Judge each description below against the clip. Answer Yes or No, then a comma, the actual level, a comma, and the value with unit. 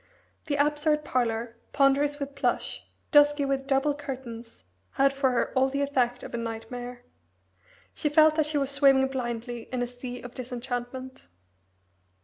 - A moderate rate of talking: Yes, average, 150 wpm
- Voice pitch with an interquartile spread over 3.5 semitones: No, narrow, 2.6 semitones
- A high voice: Yes, very high, 265 Hz